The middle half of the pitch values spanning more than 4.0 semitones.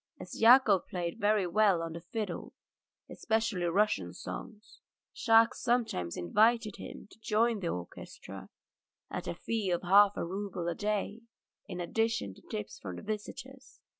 Yes: average, 4.5 semitones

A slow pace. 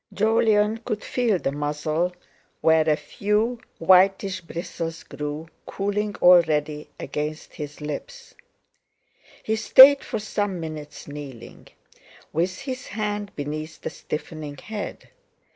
Yes: slow, 110 wpm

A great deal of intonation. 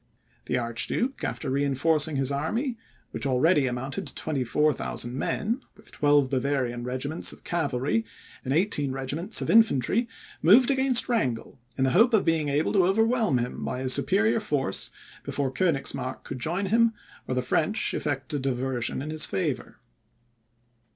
Yes: wide, 6.9 semitones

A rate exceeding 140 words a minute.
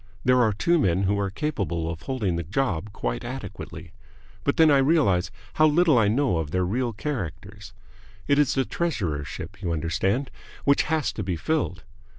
Yes: average, 175 wpm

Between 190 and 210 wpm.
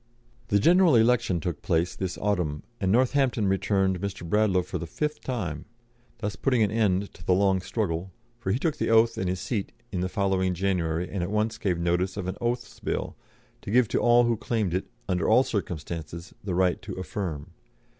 Yes: average, 195 wpm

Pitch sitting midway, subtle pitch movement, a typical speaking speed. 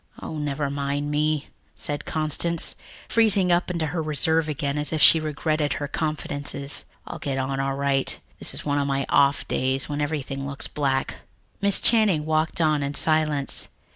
Yes: medium, 150 Hz; narrow, 2.0 semitones; average, 170 wpm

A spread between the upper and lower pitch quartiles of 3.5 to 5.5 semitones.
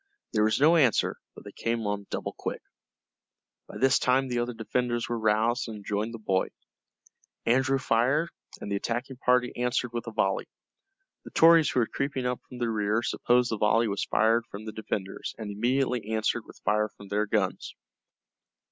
No: average, 2.7 semitones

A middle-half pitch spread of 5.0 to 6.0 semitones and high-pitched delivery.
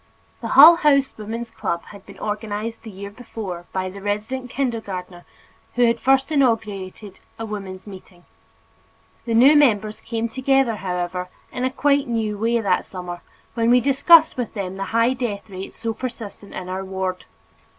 No: average, 4.4 semitones; high, 220 Hz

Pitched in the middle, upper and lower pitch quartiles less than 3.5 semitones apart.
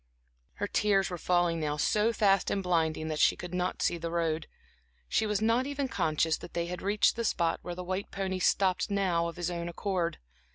Yes: medium, 180 Hz; average, 2.9 semitones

